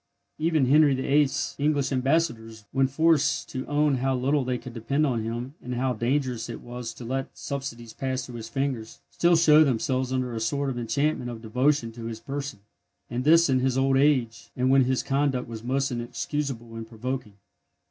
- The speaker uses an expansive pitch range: No, average, 2.9 semitones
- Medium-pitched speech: No, low, 130 Hz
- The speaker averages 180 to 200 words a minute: Yes, average, 190 wpm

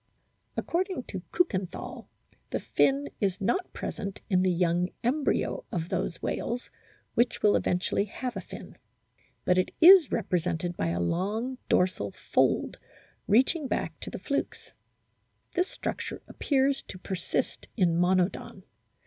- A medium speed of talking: No, slow, 130 wpm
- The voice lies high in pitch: Yes, high, 195 Hz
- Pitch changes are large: Yes, wide, 6.7 semitones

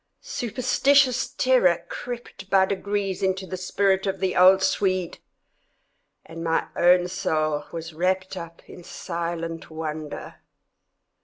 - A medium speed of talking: No, slow, 115 wpm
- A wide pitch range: No, narrow, 2.6 semitones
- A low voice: No, medium, 185 Hz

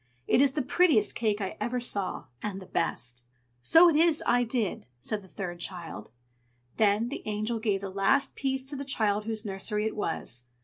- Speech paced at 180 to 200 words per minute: Yes, average, 190 wpm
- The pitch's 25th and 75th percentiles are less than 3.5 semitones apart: No, average, 4.5 semitones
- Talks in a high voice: Yes, high, 215 Hz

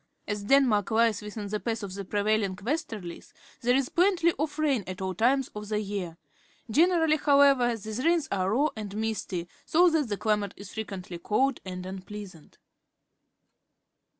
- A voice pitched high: Yes, high, 215 Hz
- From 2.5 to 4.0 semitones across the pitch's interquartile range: No, wide, 5.5 semitones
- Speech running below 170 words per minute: Yes, average, 160 wpm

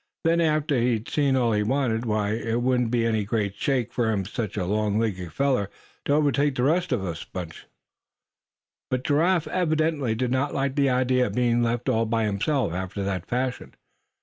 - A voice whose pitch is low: Yes, low, 120 Hz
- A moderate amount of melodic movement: Yes, average, 4.5 semitones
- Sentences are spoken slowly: No, average, 185 wpm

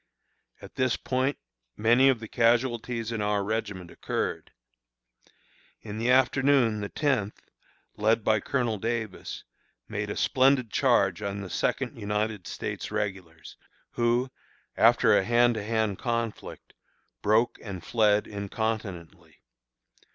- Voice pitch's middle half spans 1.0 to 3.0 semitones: Yes, narrow, 2.6 semitones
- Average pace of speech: No, slow, 120 wpm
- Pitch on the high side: No, low, 110 Hz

